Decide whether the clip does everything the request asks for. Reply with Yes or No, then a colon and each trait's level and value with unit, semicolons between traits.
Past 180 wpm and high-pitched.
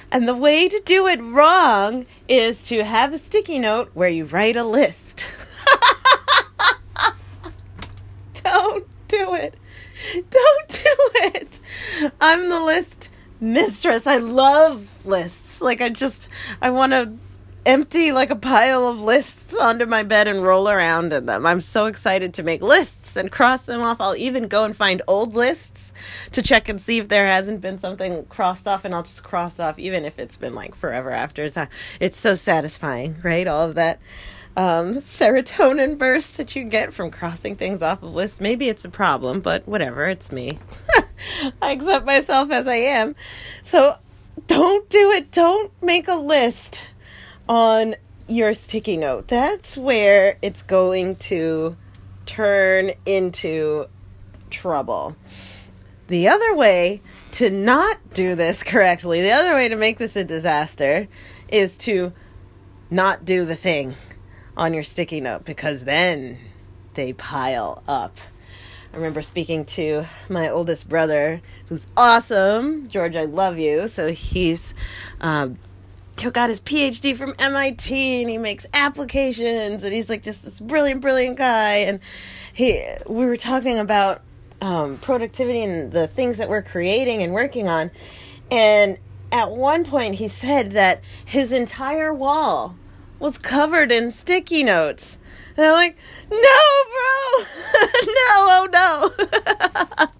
No: average, 150 wpm; high, 210 Hz